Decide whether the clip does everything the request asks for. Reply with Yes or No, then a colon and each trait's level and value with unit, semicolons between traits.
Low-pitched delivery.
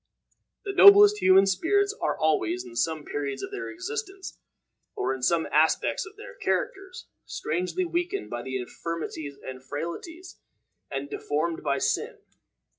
No: medium, 170 Hz